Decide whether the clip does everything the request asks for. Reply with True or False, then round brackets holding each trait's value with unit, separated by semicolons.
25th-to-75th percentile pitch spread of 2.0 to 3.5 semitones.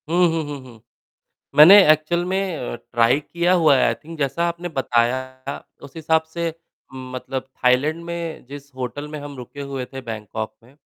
False (4.4 semitones)